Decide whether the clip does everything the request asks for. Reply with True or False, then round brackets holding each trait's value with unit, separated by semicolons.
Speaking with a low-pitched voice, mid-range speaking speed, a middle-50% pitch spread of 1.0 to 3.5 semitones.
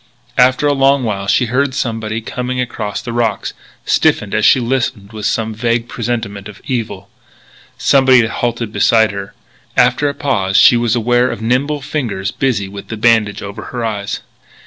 True (115 Hz; 170 wpm; 3.2 semitones)